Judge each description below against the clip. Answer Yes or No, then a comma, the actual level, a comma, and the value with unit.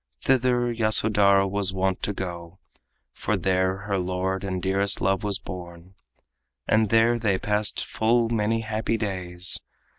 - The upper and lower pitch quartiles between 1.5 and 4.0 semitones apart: Yes, average, 2.8 semitones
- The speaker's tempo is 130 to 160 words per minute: Yes, average, 140 wpm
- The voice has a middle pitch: No, low, 100 Hz